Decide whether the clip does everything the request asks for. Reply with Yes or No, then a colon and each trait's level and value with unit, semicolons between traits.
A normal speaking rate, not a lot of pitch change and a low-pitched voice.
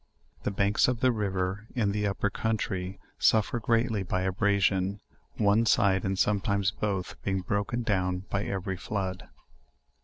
Yes: average, 145 wpm; narrow, 2.2 semitones; low, 100 Hz